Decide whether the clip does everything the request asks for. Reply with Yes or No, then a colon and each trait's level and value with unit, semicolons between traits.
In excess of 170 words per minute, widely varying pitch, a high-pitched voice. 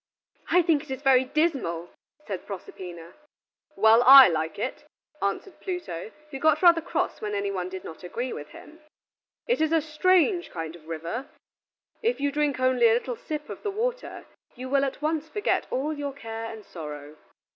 Yes: average, 180 wpm; wide, 8.6 semitones; very high, 260 Hz